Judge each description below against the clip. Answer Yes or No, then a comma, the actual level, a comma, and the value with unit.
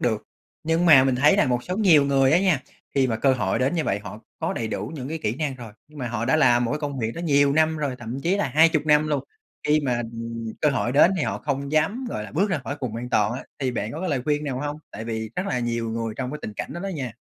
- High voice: No, low, 135 Hz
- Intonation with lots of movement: No, average, 4.4 semitones